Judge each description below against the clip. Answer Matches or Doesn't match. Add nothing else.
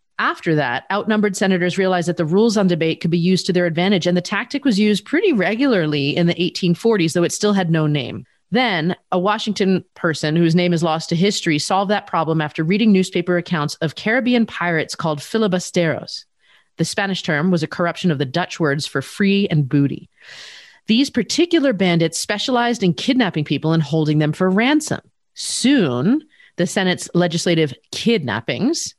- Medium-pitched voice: Matches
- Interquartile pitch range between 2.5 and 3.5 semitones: Doesn't match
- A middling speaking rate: Matches